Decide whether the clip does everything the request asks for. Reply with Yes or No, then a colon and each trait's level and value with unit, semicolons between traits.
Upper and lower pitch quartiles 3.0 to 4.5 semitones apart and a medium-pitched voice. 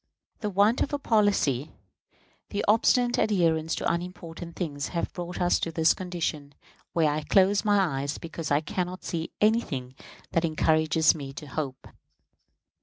Yes: average, 4.1 semitones; medium, 170 Hz